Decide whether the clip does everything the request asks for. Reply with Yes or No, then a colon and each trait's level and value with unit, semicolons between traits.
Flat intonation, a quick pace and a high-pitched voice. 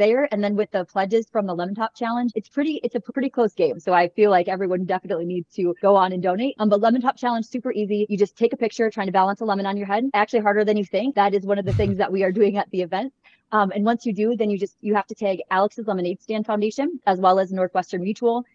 No: average, 3.1 semitones; fast, 290 wpm; high, 205 Hz